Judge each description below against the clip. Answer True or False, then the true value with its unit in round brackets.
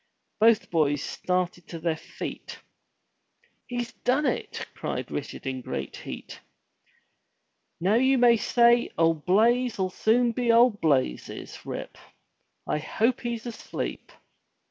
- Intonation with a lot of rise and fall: True (6.4 semitones)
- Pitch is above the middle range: True (220 Hz)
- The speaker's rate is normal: False (120 wpm)